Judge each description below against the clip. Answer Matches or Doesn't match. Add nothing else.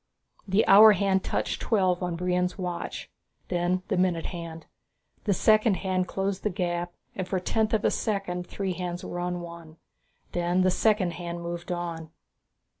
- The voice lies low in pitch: Doesn't match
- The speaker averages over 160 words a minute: Matches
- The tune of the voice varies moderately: Doesn't match